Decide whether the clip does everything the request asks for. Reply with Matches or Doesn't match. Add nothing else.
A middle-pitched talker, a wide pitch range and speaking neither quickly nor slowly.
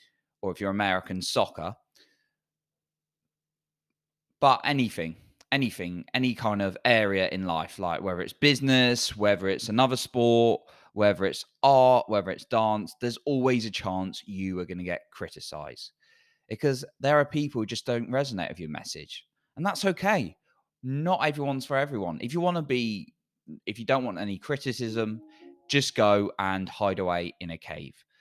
Doesn't match